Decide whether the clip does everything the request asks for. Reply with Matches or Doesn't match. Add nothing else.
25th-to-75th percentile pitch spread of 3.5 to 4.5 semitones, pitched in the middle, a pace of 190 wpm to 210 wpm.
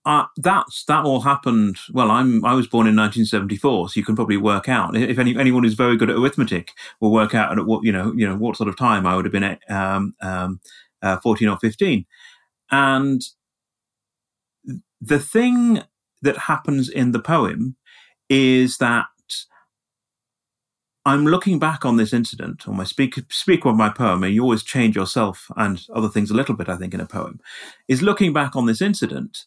Doesn't match